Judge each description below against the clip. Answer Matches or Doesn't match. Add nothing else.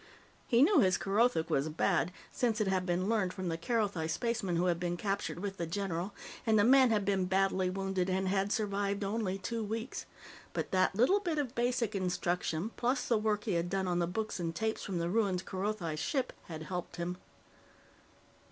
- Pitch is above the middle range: Matches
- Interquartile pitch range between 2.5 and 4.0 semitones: Matches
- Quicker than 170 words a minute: Matches